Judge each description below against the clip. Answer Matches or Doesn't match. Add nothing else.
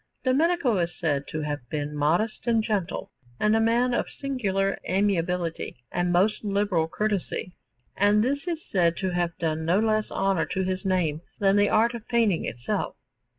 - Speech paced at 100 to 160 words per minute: Doesn't match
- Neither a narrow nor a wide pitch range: Matches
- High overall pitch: Matches